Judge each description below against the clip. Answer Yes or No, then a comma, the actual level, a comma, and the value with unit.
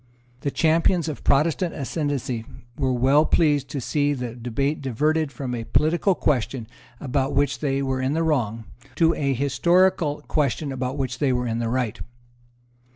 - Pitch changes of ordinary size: Yes, average, 3.2 semitones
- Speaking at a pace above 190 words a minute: No, average, 160 wpm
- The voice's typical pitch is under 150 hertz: Yes, medium, 140 Hz